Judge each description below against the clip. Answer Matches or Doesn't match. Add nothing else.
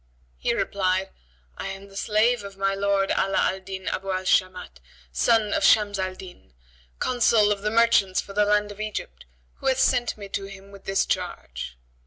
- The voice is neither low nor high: Doesn't match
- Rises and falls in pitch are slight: Matches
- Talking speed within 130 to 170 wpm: Doesn't match